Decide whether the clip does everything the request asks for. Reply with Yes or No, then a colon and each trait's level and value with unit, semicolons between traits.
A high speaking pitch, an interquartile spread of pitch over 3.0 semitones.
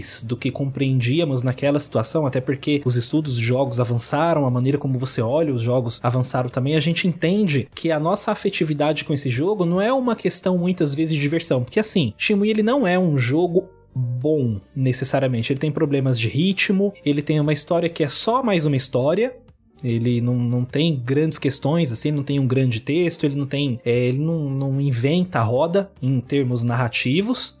No: medium, 140 Hz; average, 4.5 semitones